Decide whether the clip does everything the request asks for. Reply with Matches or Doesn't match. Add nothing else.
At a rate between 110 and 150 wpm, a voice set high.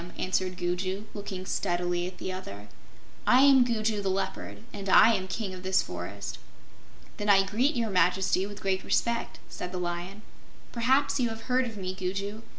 Doesn't match